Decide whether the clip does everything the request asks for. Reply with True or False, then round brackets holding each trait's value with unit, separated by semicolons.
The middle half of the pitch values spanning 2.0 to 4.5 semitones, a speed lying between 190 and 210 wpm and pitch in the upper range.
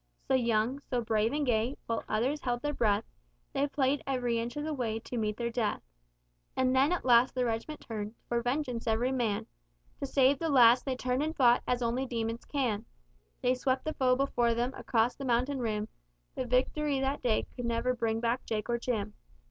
True (2.5 semitones; 205 wpm; 245 Hz)